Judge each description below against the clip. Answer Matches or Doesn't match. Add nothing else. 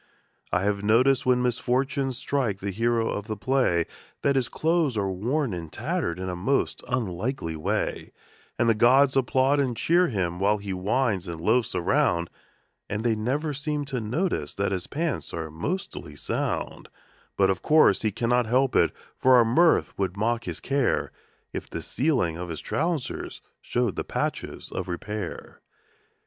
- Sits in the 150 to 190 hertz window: Doesn't match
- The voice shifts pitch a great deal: Matches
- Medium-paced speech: Matches